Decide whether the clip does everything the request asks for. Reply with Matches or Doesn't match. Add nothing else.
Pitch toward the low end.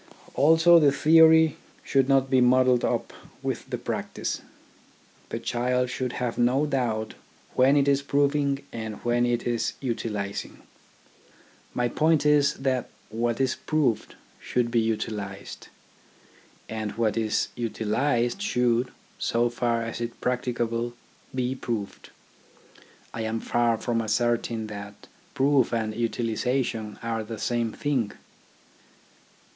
Matches